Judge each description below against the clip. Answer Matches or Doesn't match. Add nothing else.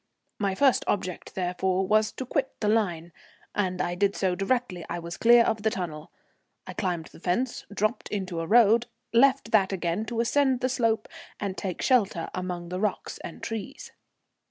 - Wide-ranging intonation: Doesn't match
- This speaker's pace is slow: Doesn't match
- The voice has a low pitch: Doesn't match